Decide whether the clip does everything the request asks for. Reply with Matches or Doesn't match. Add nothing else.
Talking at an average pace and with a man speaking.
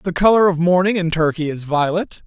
Doesn't match